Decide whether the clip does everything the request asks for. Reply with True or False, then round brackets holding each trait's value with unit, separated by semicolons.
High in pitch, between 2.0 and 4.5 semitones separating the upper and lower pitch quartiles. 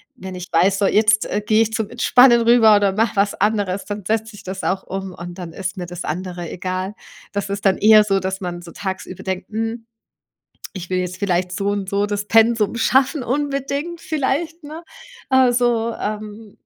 True (205 Hz; 3.5 semitones)